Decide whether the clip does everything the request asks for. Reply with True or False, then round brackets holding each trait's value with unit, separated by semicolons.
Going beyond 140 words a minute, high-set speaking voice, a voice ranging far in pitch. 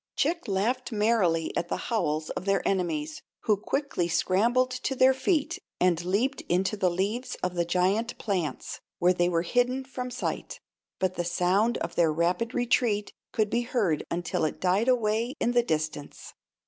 True (170 wpm; 200 Hz; 5.7 semitones)